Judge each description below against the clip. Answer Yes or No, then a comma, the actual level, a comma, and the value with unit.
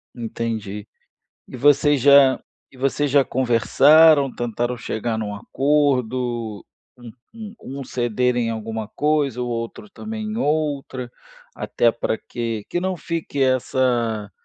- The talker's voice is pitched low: Yes, low, 125 Hz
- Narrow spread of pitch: No, average, 4.0 semitones